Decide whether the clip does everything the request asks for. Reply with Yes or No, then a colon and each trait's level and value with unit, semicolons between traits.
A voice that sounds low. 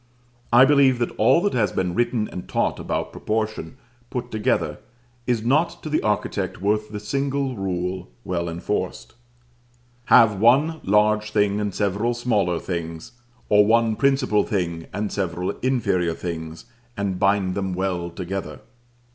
Yes: low, 105 Hz